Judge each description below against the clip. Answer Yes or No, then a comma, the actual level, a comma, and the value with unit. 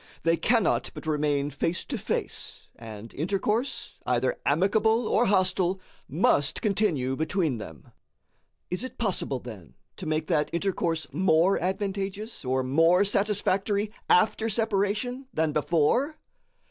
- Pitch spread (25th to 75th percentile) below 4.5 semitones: No, wide, 5.4 semitones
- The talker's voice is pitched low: No, medium, 185 Hz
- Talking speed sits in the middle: No, slow, 120 wpm